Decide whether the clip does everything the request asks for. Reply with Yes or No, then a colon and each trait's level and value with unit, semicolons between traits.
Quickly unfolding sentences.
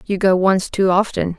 Yes: fast, 215 wpm